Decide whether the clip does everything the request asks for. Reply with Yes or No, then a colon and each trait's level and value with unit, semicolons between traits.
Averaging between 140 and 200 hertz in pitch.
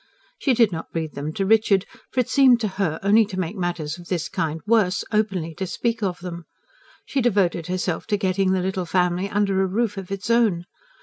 Yes: high, 190 Hz